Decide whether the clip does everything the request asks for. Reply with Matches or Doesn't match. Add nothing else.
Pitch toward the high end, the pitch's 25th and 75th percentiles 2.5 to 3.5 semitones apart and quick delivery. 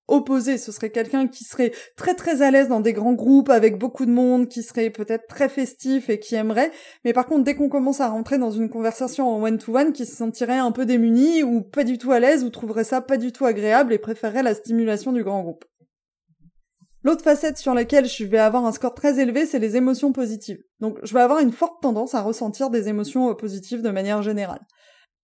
Matches